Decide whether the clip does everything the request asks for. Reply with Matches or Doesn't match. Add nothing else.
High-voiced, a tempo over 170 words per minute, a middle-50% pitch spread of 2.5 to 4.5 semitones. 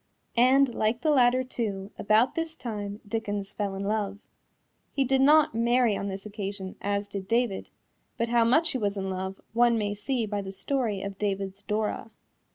Matches